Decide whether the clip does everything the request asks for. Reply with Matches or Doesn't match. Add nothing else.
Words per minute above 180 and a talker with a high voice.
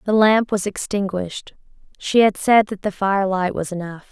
Doesn't match